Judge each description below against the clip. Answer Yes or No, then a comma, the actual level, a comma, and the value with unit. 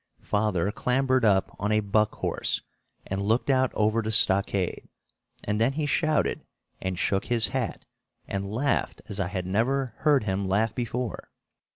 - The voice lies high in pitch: No, low, 110 Hz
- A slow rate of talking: No, average, 160 wpm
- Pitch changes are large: No, average, 4.1 semitones